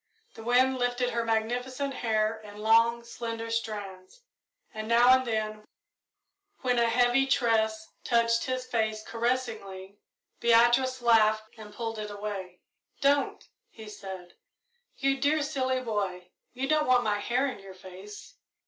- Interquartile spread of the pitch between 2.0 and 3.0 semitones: Yes, average, 2.7 semitones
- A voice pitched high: Yes, high, 230 Hz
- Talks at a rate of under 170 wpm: Yes, average, 140 wpm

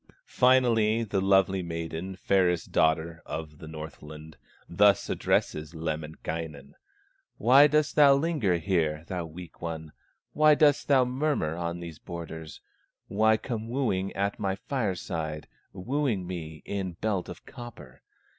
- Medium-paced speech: No, slow, 120 wpm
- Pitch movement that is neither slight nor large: No, wide, 5.9 semitones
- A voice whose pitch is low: Yes, very low, 90 Hz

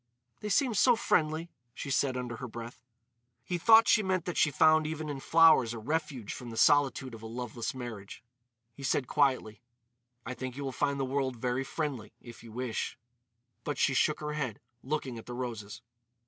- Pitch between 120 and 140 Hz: Yes, low, 135 Hz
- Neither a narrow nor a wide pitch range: Yes, average, 4.3 semitones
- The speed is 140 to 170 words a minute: No, average, 190 wpm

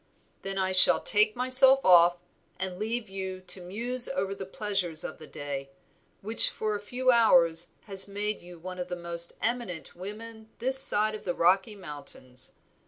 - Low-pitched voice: No, high, 195 Hz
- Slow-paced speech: No, average, 170 wpm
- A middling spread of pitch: Yes, average, 3.9 semitones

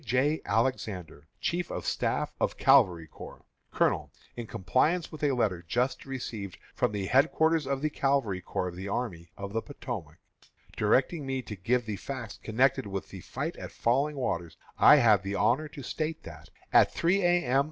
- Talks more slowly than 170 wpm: No, average, 180 wpm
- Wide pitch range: Yes, wide, 6.1 semitones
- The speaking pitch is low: Yes, low, 125 Hz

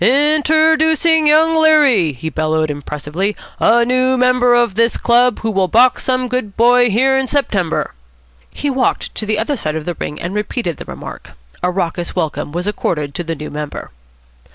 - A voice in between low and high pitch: No, high, 230 Hz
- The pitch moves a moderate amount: No, wide, 7.2 semitones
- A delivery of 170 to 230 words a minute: Yes, average, 190 wpm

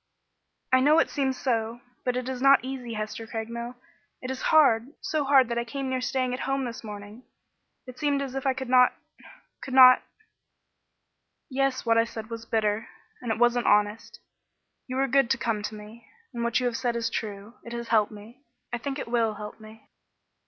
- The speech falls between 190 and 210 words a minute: Yes, fast, 205 wpm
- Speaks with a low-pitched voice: No, high, 240 Hz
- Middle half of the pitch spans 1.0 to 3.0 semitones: Yes, average, 2.7 semitones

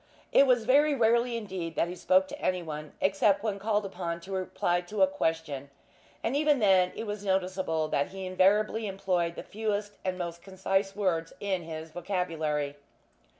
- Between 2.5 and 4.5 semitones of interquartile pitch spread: Yes, average, 3.5 semitones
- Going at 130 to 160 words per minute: No, average, 170 wpm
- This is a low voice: No, high, 190 Hz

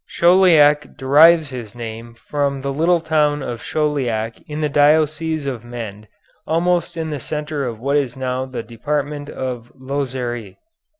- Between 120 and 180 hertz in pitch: Yes, medium, 140 Hz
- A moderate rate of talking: Yes, average, 145 wpm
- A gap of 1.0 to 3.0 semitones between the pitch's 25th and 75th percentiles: No, average, 3.9 semitones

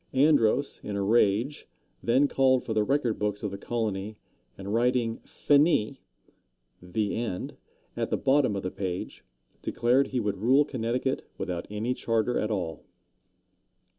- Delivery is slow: No, average, 145 wpm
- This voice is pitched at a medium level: No, low, 115 Hz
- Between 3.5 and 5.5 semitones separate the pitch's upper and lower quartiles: Yes, average, 4.1 semitones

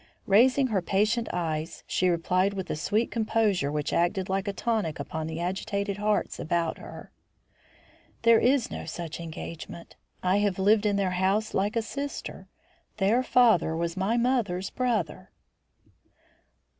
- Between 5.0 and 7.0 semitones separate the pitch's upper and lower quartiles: No, average, 4.2 semitones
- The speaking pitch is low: No, high, 195 Hz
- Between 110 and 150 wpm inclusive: Yes, average, 145 wpm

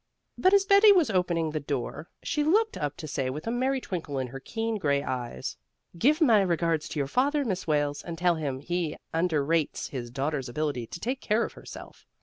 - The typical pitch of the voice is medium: Yes, medium, 165 Hz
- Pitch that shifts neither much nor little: No, wide, 8.3 semitones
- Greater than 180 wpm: Yes, fast, 205 wpm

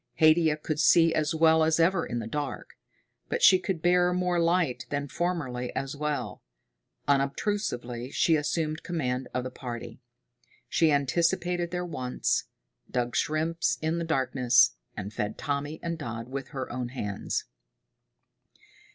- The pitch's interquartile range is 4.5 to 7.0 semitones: Yes, average, 4.8 semitones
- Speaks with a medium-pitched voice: Yes, medium, 150 Hz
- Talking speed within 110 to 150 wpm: Yes, average, 140 wpm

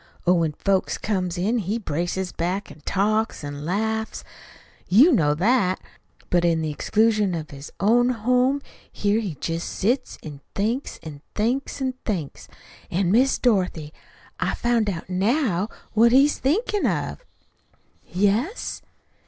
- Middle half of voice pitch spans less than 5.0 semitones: No, wide, 5.5 semitones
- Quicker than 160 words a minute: No, average, 140 wpm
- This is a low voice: No, high, 205 Hz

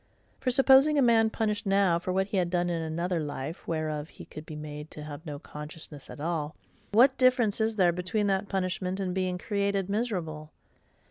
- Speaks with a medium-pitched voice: Yes, medium, 180 Hz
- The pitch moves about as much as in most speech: Yes, average, 4.7 semitones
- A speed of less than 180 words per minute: No, average, 195 wpm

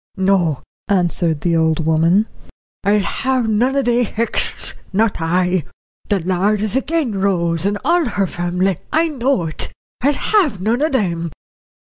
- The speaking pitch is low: No, high, 200 Hz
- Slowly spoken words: No, average, 150 wpm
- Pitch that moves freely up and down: Yes, wide, 5.8 semitones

